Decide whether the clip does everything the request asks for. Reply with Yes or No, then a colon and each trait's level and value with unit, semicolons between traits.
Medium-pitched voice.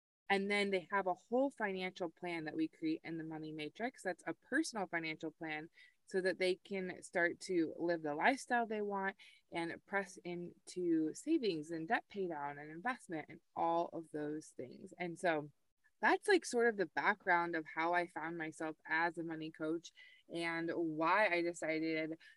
Yes: medium, 175 Hz